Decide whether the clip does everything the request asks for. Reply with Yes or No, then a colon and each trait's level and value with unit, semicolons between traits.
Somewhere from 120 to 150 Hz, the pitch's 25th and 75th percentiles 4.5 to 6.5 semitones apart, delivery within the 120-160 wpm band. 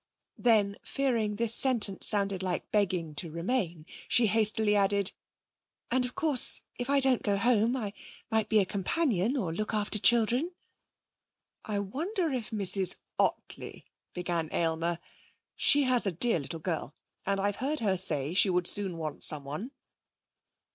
No: high, 205 Hz; average, 5.1 semitones; average, 155 wpm